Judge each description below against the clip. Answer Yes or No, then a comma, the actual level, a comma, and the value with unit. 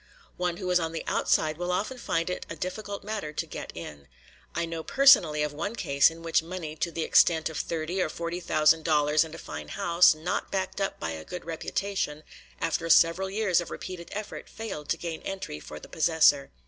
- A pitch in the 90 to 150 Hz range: No, medium, 165 Hz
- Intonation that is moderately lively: Yes, average, 3.0 semitones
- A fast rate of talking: Yes, fast, 210 wpm